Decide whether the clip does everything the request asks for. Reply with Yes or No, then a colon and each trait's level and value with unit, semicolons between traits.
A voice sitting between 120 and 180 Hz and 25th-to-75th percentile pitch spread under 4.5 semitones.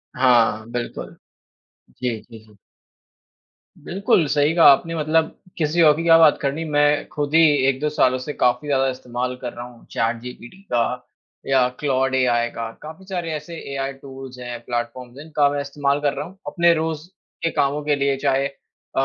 Yes: medium, 140 Hz; average, 3.6 semitones